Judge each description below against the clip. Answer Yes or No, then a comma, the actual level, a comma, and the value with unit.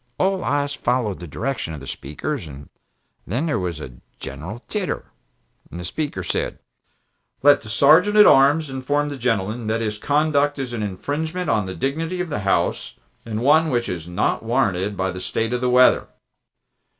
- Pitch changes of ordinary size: No, wide, 7.0 semitones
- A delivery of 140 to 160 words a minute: No, average, 175 wpm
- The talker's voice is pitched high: No, low, 125 Hz